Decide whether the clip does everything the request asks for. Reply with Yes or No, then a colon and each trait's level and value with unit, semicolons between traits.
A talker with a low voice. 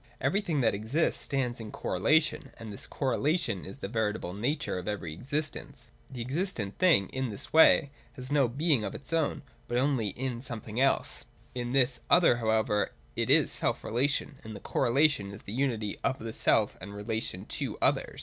Yes: low, 120 Hz